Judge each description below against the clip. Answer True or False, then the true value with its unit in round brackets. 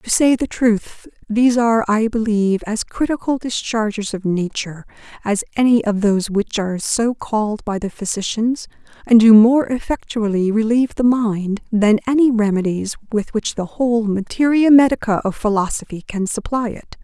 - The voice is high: True (220 Hz)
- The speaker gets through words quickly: False (160 wpm)